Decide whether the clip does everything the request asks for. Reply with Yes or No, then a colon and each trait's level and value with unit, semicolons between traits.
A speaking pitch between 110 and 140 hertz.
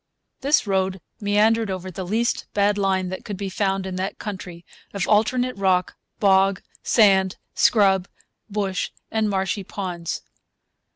No: high, 195 Hz